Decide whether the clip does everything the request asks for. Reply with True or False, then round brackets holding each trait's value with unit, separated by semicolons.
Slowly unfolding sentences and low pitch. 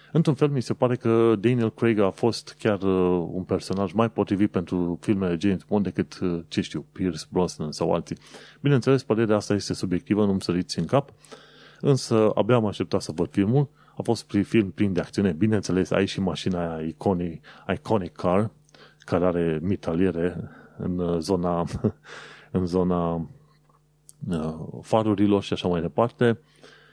False (160 wpm; 100 Hz)